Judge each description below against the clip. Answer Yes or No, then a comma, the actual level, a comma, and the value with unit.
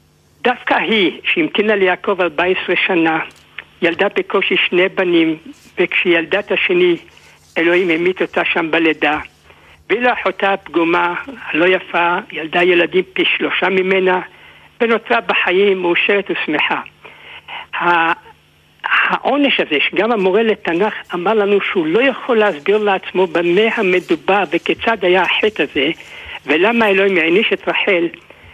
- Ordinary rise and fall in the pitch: Yes, average, 3.8 semitones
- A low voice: No, high, 190 Hz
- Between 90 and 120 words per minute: Yes, average, 115 wpm